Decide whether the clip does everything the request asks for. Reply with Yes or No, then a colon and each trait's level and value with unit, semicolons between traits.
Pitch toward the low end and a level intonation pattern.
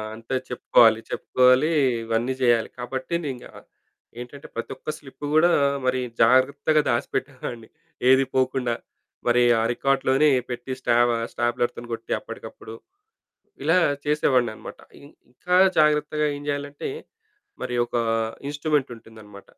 No: low, 130 Hz; average, 3.1 semitones